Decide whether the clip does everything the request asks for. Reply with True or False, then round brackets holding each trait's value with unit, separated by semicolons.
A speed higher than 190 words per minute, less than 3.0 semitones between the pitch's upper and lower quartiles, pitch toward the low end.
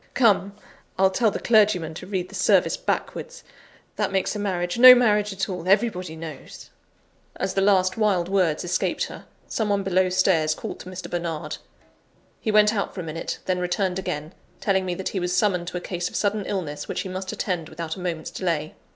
False (205 wpm; 2.4 semitones; 185 Hz)